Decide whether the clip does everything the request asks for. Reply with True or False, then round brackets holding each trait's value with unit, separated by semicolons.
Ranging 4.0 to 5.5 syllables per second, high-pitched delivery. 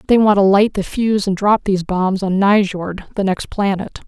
True (4.8 syllables/s; 195 Hz)